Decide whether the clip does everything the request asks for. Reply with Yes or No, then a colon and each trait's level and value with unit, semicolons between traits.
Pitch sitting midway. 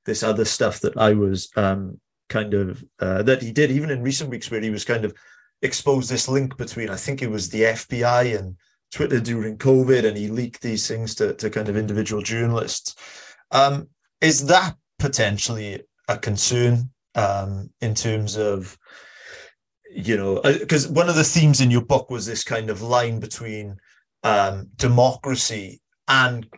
No: low, 115 Hz